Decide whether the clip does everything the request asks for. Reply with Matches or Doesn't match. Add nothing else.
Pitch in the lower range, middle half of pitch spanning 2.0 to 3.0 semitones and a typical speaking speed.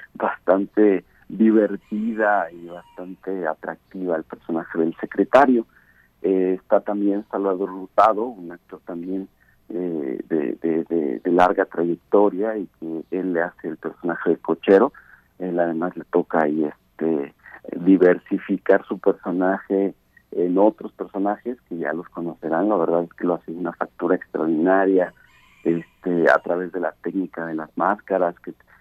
Matches